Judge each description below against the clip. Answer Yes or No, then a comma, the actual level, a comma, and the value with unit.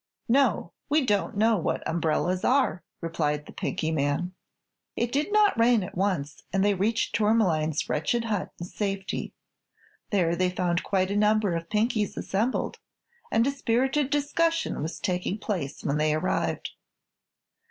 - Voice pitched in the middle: No, high, 200 Hz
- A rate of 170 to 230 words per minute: No, average, 150 wpm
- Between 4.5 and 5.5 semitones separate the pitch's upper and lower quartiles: Yes, average, 5.2 semitones